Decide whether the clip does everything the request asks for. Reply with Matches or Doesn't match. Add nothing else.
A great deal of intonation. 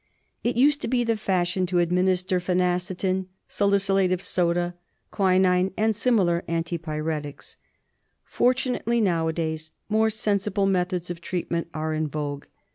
Doesn't match